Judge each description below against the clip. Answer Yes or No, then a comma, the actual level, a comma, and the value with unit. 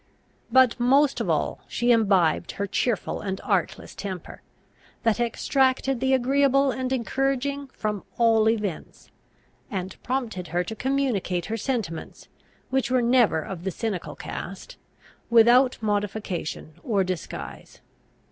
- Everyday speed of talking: No, slow, 125 wpm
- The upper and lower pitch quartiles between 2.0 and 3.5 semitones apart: No, average, 5.1 semitones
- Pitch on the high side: Yes, high, 230 Hz